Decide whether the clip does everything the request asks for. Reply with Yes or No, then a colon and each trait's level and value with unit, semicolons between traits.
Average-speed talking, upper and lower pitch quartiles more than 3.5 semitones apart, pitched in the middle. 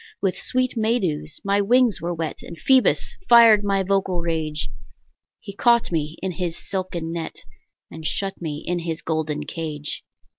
Yes: average, 160 wpm; average, 4.0 semitones; medium, 175 Hz